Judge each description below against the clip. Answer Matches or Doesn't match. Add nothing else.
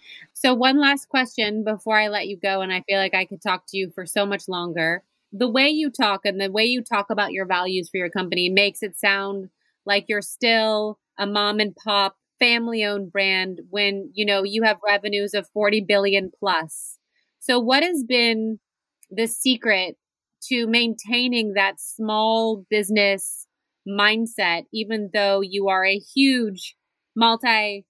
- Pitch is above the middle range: Matches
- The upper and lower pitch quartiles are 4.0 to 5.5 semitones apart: Doesn't match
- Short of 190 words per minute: Matches